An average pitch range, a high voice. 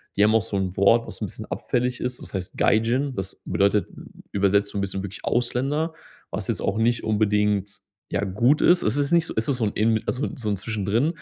No: average, 3.6 semitones; low, 110 Hz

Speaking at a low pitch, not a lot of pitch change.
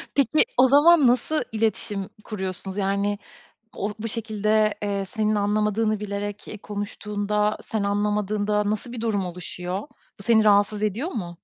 No: high, 210 Hz; narrow, 1.4 semitones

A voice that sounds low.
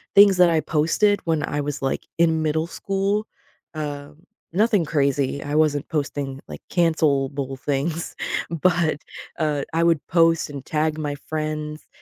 No: medium, 155 Hz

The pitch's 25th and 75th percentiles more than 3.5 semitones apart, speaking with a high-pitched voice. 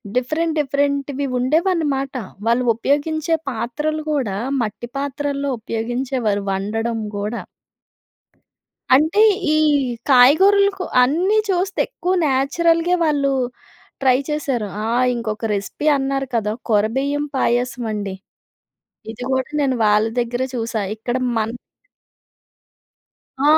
Yes: average, 4.6 semitones; very high, 270 Hz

